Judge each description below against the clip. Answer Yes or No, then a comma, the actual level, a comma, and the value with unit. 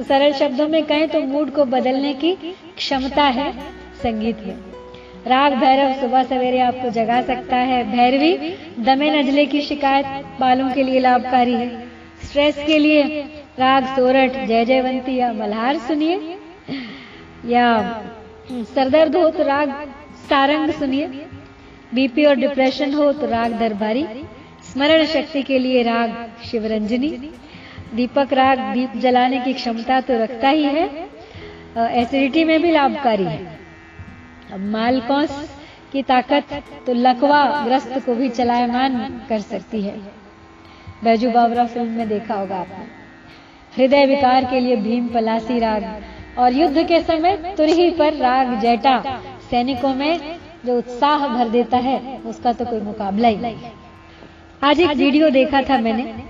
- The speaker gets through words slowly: No, average, 140 wpm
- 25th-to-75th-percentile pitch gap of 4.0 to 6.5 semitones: No, average, 3.2 semitones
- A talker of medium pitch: No, very high, 260 Hz